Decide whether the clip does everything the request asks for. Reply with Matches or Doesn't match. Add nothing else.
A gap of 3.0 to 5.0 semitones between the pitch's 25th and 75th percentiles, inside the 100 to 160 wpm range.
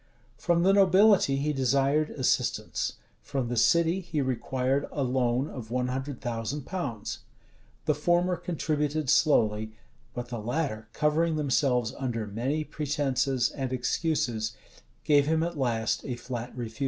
Matches